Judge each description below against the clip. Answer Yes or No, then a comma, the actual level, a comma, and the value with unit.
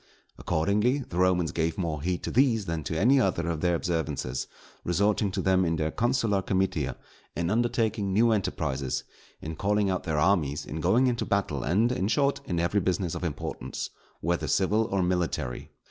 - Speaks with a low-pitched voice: Yes, very low, 95 Hz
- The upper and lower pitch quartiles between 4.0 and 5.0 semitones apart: Yes, average, 4.3 semitones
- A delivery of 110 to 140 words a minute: No, average, 175 wpm